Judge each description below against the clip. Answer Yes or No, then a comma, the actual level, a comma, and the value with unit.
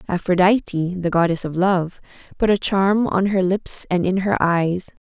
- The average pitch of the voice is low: No, medium, 185 Hz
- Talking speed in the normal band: Yes, average, 175 wpm